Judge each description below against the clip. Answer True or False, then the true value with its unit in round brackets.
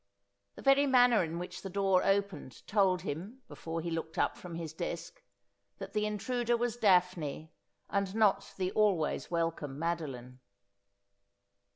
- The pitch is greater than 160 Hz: True (185 Hz)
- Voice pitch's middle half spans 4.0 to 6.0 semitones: True (4.4 semitones)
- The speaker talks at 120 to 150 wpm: True (145 wpm)